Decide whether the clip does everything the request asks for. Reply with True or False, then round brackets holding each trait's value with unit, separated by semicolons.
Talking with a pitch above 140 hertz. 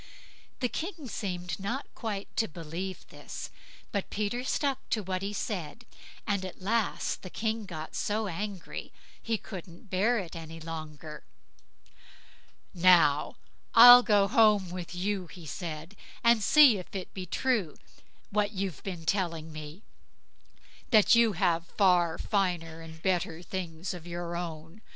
True (185 Hz)